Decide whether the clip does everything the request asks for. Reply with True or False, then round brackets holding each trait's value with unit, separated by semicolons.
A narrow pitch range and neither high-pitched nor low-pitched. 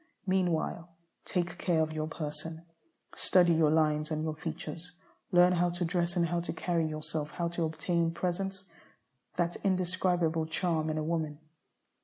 True (2.0 semitones; 170 Hz)